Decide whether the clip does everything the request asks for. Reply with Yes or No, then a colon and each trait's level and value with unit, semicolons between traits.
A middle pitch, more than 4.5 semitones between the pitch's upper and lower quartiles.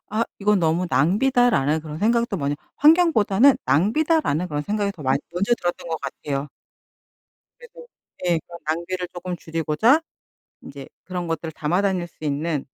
Yes: medium, 175 Hz; wide, 5.5 semitones